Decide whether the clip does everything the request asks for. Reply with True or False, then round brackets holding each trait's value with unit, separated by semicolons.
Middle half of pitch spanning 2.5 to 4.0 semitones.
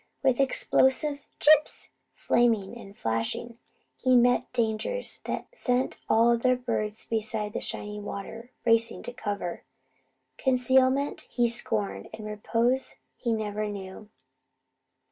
True (3.3 semitones)